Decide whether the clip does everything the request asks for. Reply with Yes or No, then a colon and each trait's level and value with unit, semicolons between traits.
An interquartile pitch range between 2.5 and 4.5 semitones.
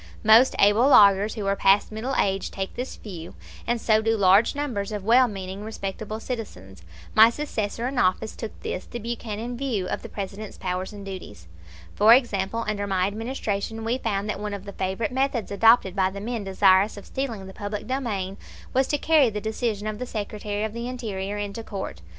Yes: average, 2.9 semitones